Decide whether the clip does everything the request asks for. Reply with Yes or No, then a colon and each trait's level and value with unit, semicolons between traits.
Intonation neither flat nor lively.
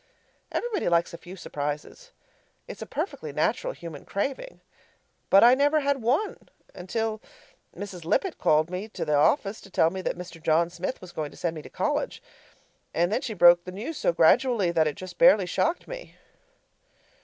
No: wide, 7.0 semitones